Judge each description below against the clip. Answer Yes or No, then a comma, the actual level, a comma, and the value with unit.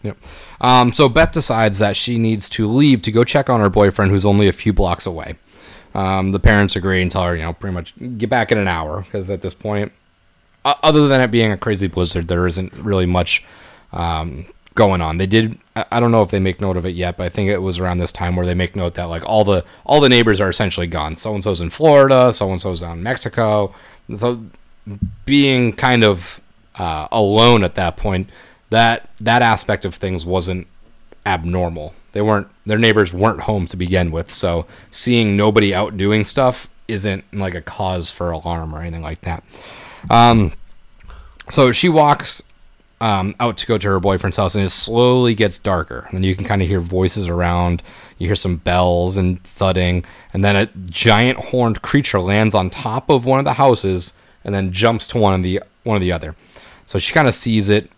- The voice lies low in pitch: Yes, low, 100 Hz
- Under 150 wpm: No, fast, 205 wpm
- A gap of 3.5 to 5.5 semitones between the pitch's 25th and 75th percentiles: Yes, average, 3.9 semitones